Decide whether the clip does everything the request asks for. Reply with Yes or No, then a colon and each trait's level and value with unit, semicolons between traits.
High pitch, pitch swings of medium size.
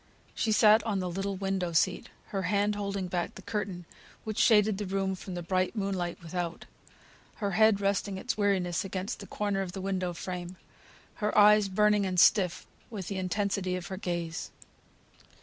No: high, 195 Hz; narrow, 2.0 semitones